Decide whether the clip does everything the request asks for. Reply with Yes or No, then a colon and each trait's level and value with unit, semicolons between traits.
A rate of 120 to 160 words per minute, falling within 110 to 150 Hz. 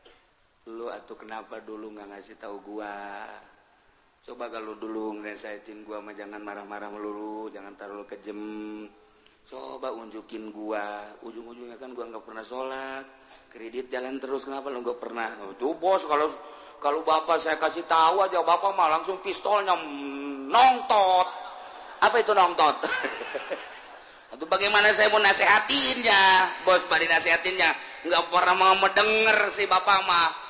Yes: fast, 140 wpm; medium, 140 Hz